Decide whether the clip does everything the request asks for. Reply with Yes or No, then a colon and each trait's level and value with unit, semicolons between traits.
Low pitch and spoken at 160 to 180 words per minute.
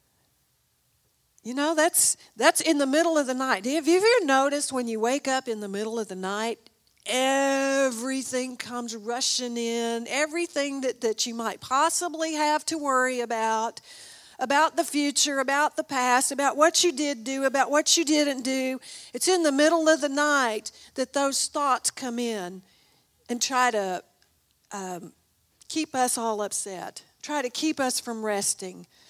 No: very high, 265 Hz; average, 165 wpm